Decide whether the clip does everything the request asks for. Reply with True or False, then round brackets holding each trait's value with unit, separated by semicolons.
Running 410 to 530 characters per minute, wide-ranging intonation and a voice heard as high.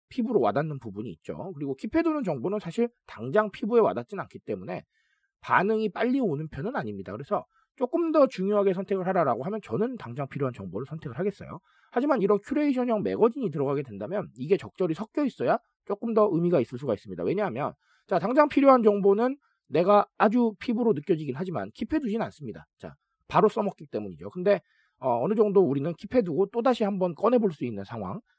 True (430 characters per minute; 6.2 semitones; 205 Hz)